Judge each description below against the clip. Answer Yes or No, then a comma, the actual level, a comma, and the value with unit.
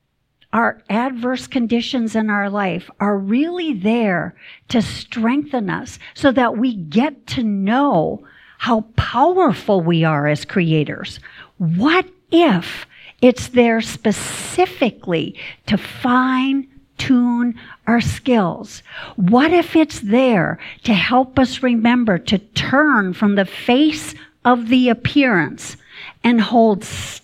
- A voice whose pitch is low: No, high, 235 Hz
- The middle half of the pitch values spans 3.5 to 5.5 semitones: Yes, average, 4.1 semitones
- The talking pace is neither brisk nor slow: No, slow, 115 wpm